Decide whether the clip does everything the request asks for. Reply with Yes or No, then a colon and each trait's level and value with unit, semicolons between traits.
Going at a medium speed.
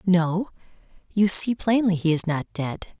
Yes: average, 160 wpm